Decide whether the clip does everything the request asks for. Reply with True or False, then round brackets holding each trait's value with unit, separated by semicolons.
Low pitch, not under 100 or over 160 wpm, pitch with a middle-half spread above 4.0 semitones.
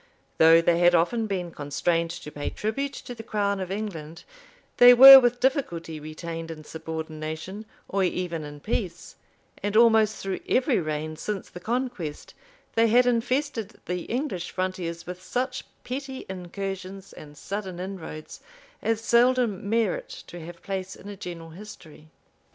False (190 Hz; 150 wpm; 5.4 semitones)